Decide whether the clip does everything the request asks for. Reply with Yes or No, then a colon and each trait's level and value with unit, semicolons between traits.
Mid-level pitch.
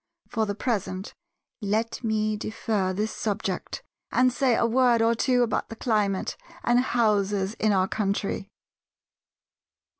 No: high, 215 Hz